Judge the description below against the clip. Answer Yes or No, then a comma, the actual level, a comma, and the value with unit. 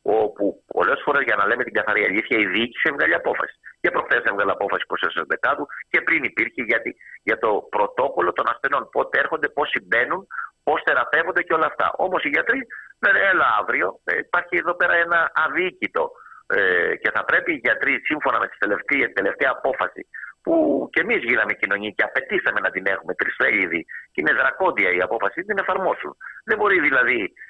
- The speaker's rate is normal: No, fast, 175 wpm